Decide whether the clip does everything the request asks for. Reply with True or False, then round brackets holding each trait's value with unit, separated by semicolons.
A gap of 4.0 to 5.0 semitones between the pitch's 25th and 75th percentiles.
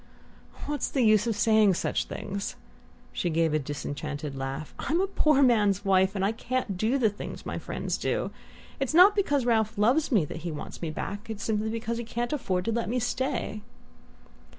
True (4.7 semitones)